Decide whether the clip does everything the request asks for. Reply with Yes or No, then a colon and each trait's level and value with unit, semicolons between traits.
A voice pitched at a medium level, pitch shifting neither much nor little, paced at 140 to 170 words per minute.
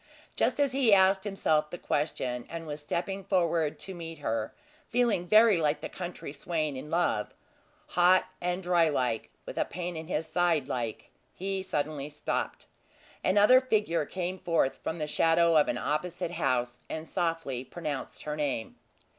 Yes: medium, 165 Hz; average, 3.8 semitones; average, 165 wpm